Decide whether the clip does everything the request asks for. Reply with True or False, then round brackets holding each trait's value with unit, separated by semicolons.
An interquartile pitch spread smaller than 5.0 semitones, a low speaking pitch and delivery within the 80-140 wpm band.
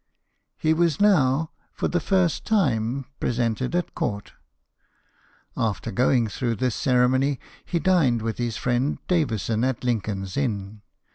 False (5.6 semitones; 125 Hz; 135 wpm)